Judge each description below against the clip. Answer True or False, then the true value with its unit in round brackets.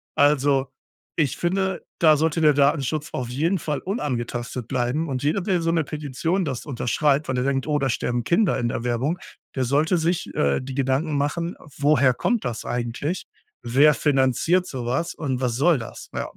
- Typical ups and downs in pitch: True (4.1 semitones)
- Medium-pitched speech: True (145 Hz)